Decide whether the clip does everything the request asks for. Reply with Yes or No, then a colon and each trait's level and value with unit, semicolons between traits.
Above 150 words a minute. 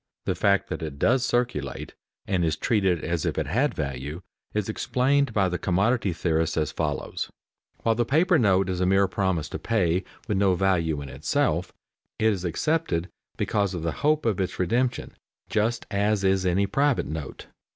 Yes: average, 180 wpm